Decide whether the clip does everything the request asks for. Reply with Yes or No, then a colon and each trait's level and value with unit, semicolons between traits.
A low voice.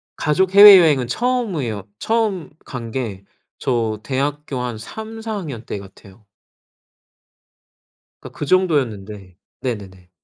Yes: low, 130 Hz